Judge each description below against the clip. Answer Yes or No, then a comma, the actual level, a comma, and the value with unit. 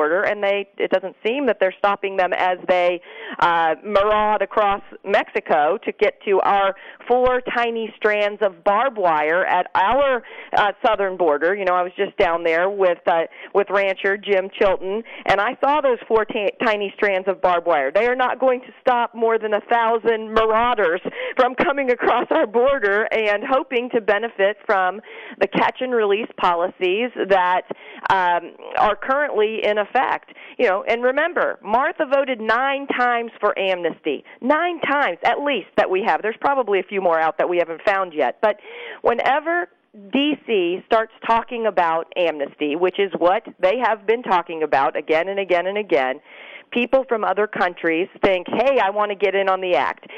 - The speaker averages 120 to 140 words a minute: No, average, 175 wpm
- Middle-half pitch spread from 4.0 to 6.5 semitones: Yes, average, 4.5 semitones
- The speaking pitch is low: No, high, 210 Hz